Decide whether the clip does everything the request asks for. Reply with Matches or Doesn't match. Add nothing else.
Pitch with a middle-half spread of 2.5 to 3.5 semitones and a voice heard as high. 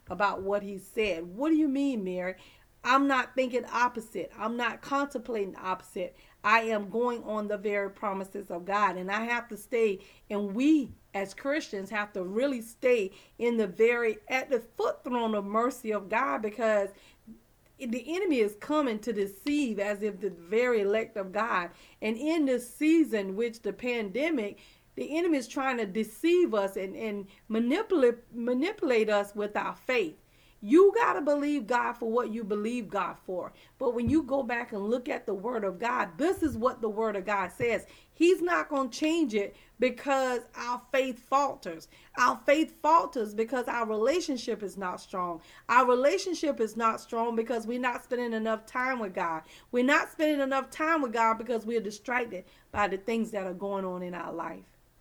Doesn't match